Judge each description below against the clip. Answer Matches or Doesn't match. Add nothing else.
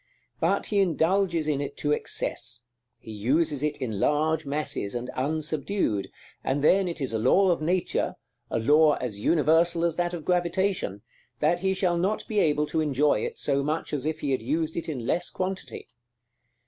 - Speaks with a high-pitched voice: Doesn't match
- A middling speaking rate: Matches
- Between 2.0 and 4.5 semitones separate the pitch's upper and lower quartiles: Matches